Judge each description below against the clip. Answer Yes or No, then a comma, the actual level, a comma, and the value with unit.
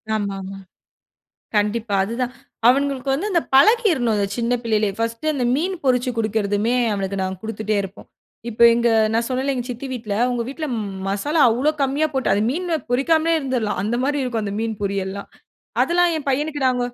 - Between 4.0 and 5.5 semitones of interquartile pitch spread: Yes, average, 4.7 semitones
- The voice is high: Yes, high, 245 Hz